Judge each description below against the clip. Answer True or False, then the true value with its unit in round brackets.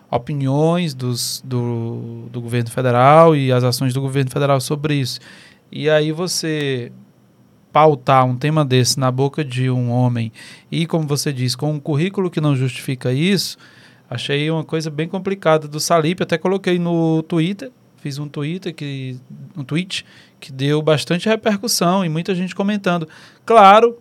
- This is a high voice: False (150 Hz)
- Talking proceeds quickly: False (155 wpm)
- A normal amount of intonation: True (4.5 semitones)